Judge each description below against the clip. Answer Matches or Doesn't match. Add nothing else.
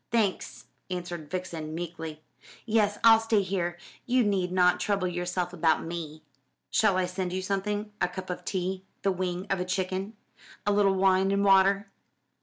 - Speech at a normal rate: Matches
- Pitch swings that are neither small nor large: Doesn't match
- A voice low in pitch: Doesn't match